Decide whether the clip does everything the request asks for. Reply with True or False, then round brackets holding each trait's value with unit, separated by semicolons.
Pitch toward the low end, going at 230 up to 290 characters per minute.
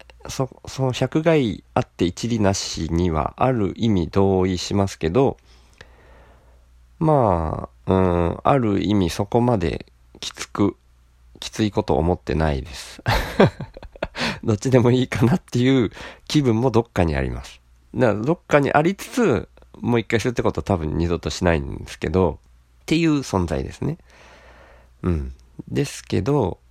True (95 Hz; 280 characters per minute)